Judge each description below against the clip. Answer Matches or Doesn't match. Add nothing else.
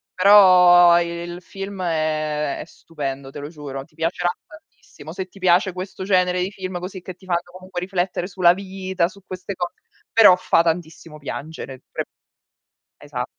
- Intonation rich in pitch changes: Doesn't match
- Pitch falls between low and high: Matches